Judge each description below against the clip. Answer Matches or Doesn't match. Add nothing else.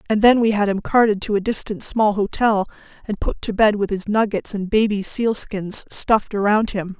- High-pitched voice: Matches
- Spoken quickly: Matches